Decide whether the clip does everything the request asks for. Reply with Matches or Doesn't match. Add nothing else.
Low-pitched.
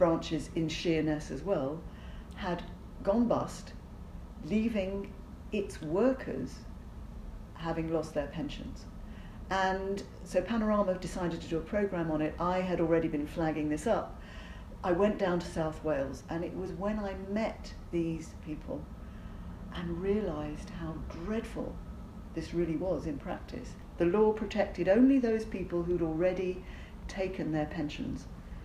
Doesn't match